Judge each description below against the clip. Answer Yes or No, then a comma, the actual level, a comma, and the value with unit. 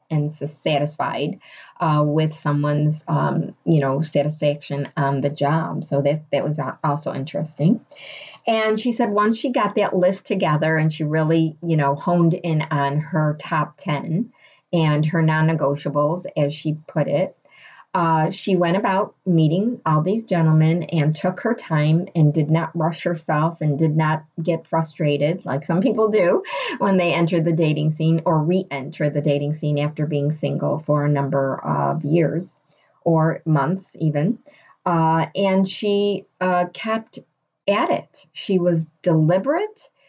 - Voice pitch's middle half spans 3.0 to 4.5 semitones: Yes, average, 3.5 semitones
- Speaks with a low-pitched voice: No, medium, 160 Hz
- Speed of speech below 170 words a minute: Yes, average, 155 wpm